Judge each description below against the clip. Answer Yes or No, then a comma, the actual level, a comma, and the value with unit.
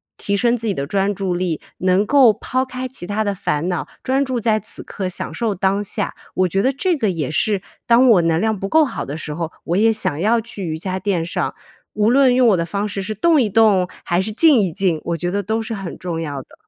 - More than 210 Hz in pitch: No, high, 200 Hz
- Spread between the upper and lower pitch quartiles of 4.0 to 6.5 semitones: Yes, average, 4.4 semitones